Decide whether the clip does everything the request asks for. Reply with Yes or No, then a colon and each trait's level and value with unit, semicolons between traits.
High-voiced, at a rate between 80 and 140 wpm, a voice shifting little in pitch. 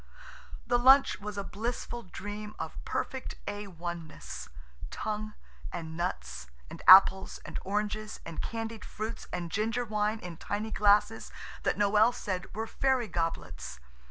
No: high, 210 Hz; slow, 135 wpm; average, 3.7 semitones